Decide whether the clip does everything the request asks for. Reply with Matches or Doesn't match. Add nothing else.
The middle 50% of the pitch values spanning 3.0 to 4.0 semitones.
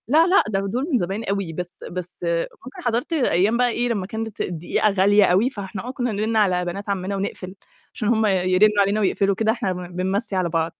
Matches